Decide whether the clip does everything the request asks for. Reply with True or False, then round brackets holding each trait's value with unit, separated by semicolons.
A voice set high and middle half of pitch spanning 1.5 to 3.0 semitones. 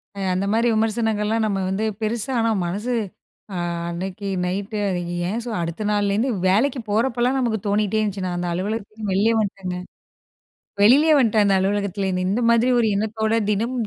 True (210 Hz; 2.7 semitones)